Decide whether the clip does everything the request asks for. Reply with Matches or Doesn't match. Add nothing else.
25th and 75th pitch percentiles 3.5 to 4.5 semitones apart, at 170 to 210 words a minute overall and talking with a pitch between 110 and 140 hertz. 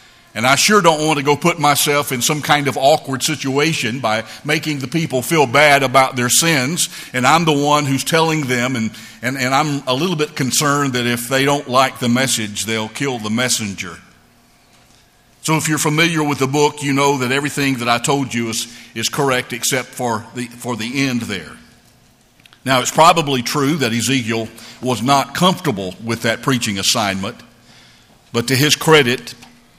Matches